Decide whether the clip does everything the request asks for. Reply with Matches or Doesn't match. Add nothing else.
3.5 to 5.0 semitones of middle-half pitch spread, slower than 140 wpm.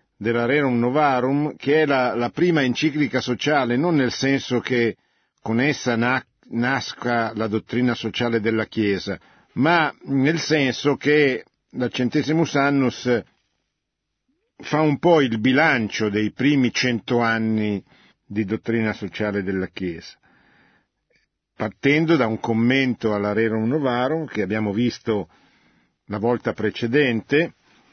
Matches